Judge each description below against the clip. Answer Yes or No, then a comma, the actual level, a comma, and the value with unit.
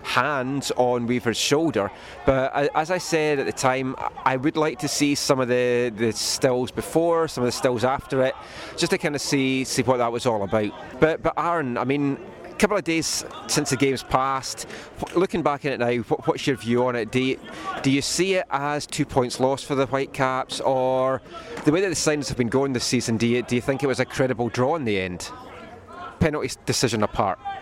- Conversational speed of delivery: No, fast, 225 wpm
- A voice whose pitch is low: Yes, low, 130 Hz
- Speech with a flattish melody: No, average, 3.0 semitones